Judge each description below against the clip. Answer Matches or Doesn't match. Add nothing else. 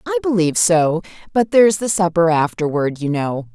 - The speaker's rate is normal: Matches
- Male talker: Doesn't match